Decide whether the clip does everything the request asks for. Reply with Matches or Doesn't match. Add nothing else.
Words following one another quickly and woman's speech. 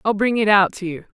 Matches